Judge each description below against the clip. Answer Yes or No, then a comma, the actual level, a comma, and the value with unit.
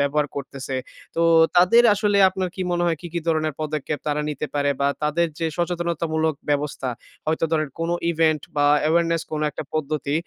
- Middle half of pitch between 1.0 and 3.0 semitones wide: Yes, narrow, 2.5 semitones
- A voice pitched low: No, medium, 155 Hz